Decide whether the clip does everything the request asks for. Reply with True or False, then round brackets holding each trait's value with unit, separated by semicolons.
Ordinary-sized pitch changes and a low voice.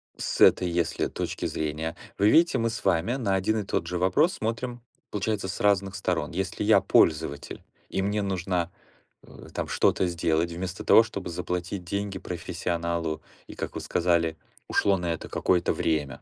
True (3.1 semitones; 90 Hz)